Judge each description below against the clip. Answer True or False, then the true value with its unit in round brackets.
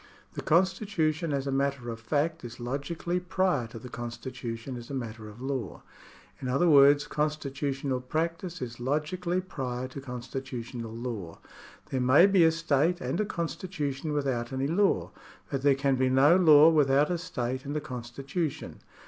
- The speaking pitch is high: False (140 Hz)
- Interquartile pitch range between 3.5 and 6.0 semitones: True (4.4 semitones)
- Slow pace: False (165 wpm)